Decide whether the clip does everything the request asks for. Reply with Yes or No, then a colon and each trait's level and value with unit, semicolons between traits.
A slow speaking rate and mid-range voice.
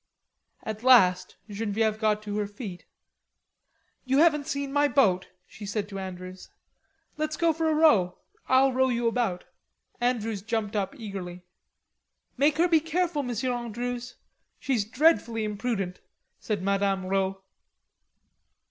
No: slow, 130 wpm; high, 225 Hz